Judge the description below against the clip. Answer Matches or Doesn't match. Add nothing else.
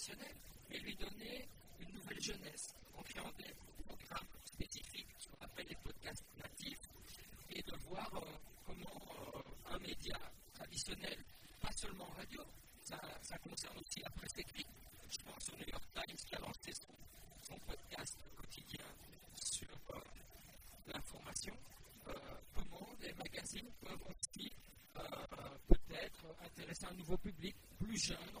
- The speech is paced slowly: Matches